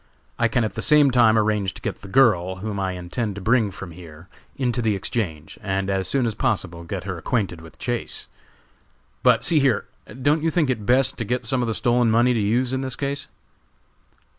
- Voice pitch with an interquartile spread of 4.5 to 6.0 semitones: Yes, average, 4.8 semitones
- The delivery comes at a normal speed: No, fast, 215 wpm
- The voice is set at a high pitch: No, low, 110 Hz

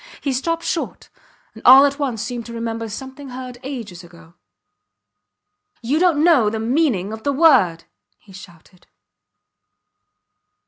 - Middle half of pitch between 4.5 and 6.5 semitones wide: Yes, average, 5.2 semitones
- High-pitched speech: Yes, high, 245 Hz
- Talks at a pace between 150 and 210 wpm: No, slow, 135 wpm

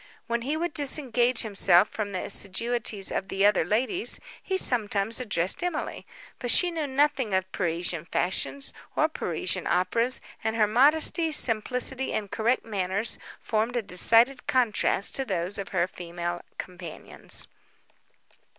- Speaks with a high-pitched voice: Yes, high, 220 Hz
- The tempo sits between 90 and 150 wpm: Yes, average, 140 wpm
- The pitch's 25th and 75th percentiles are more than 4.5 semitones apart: Yes, wide, 5.5 semitones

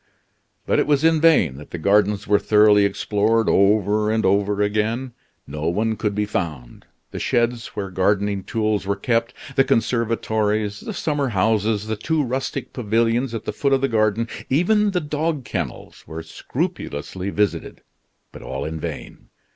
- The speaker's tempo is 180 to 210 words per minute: No, average, 165 wpm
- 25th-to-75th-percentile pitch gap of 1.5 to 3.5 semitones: Yes, average, 3.0 semitones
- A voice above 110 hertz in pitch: No, low, 105 Hz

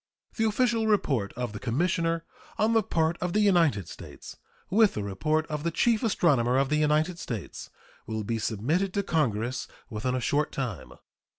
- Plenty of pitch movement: Yes, wide, 7.6 semitones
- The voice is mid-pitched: Yes, medium, 155 Hz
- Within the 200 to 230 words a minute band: No, average, 175 wpm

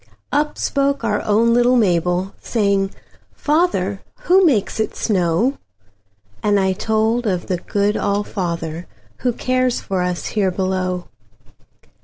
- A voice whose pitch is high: Yes, high, 200 Hz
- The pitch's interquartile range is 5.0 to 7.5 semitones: No, average, 4.5 semitones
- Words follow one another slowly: Yes, slow, 115 wpm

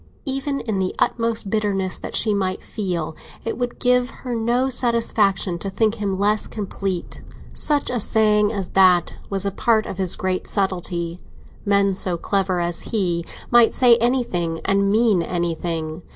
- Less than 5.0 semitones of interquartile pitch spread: Yes, average, 3.9 semitones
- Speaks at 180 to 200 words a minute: No, average, 155 wpm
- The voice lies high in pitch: Yes, high, 200 Hz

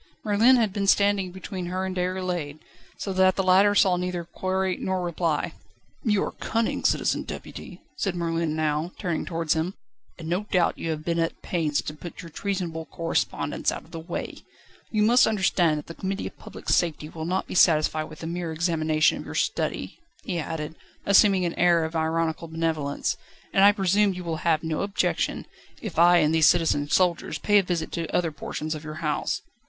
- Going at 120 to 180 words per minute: No, average, 195 wpm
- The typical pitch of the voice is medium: Yes, medium, 170 Hz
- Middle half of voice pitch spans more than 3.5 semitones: No, average, 2.8 semitones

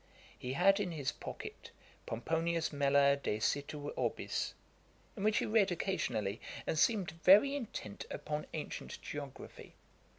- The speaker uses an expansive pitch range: Yes, wide, 5.8 semitones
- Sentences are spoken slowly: Yes, slow, 130 wpm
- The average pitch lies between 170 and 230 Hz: No, medium, 160 Hz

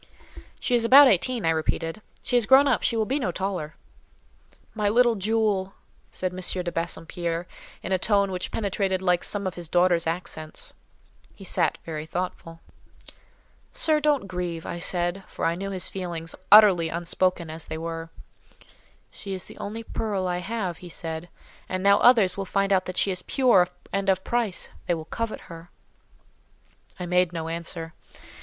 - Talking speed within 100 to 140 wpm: No, average, 175 wpm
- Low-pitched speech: No, medium, 185 Hz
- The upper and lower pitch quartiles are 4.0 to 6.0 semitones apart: No, average, 3.3 semitones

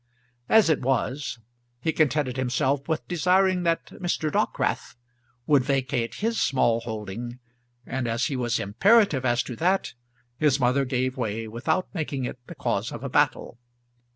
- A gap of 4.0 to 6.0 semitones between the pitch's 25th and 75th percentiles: Yes, average, 4.6 semitones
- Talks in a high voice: No, low, 135 Hz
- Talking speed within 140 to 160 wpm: Yes, average, 155 wpm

